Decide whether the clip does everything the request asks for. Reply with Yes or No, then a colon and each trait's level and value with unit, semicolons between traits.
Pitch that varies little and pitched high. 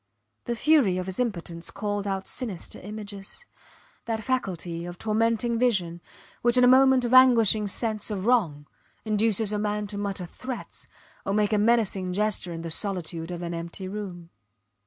No: average, 4.1 semitones; high, 205 Hz